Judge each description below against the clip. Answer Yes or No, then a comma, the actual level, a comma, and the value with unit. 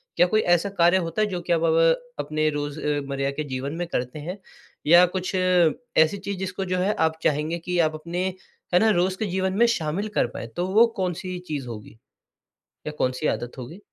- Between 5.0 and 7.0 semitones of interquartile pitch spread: No, average, 3.6 semitones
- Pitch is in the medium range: Yes, medium, 170 Hz